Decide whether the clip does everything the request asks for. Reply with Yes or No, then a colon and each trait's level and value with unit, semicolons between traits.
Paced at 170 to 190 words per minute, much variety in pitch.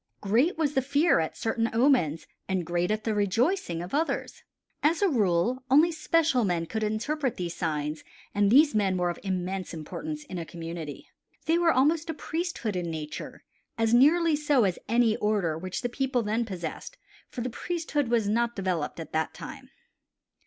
Yes: average, 175 wpm; wide, 8.4 semitones